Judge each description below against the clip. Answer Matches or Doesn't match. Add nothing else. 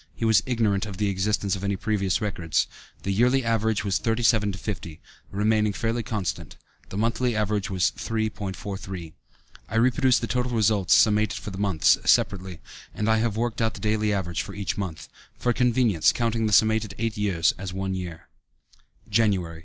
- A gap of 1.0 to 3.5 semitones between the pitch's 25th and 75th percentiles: Matches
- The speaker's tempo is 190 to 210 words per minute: Doesn't match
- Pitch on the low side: Matches